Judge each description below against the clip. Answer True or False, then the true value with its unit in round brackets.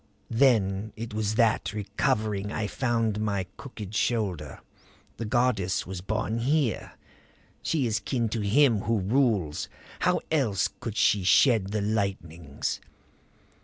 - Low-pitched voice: True (110 Hz)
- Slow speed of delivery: True (130 wpm)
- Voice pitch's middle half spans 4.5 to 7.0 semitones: False (2.9 semitones)